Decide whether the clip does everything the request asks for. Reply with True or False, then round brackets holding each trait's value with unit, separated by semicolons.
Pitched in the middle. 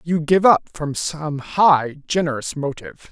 True (155 Hz)